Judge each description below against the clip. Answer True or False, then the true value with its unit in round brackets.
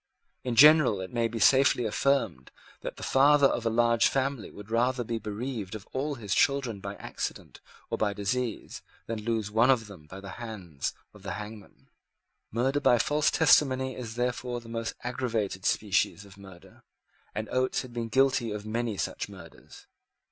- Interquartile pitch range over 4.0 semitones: False (3.7 semitones)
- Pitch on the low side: True (115 Hz)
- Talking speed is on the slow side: False (175 wpm)